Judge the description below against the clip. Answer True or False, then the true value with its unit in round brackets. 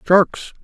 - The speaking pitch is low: False (185 Hz)